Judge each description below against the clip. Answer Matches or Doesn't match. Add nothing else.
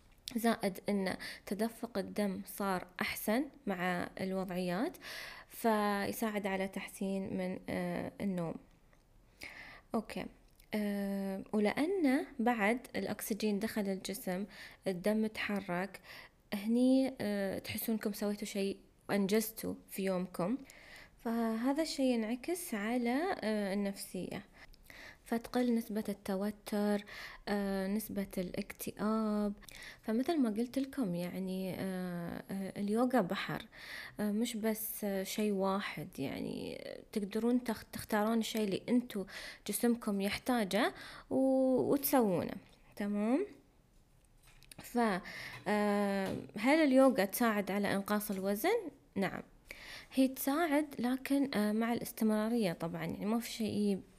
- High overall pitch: Matches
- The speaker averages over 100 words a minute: Doesn't match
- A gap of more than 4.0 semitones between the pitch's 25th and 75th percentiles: Doesn't match